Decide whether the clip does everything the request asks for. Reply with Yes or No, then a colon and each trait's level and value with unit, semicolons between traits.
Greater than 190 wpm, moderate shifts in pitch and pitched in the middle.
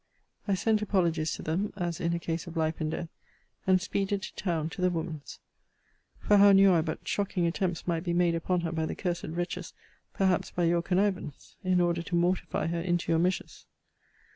No: average, 200 wpm; narrow, 2.0 semitones; medium, 175 Hz